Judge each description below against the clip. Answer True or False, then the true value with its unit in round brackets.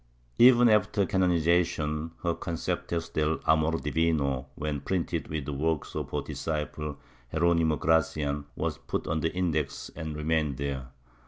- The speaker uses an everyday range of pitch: False (1.9 semitones)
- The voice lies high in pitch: False (80 Hz)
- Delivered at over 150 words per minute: False (140 wpm)